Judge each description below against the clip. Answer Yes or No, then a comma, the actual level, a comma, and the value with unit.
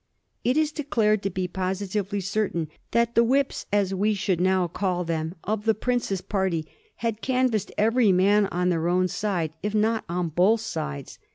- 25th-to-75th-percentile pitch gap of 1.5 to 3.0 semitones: No, average, 3.5 semitones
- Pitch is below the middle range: No, high, 200 Hz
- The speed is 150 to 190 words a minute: Yes, average, 175 wpm